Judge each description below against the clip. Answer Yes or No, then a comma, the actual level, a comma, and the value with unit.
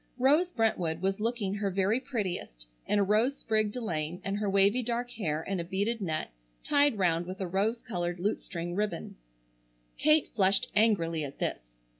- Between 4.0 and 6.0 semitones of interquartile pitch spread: Yes, average, 4.5 semitones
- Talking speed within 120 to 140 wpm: No, average, 175 wpm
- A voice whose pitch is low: No, high, 200 Hz